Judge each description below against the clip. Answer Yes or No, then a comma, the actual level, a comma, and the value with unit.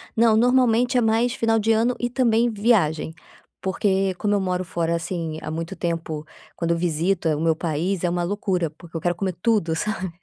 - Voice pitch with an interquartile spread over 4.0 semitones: Yes, average, 5.0 semitones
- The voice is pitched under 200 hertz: Yes, medium, 185 Hz